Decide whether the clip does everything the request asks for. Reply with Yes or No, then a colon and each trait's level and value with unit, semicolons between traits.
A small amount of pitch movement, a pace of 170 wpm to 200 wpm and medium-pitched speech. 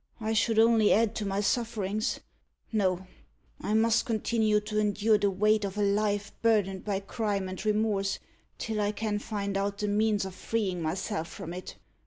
No: narrow, 1.7 semitones; average, 175 wpm; high, 210 Hz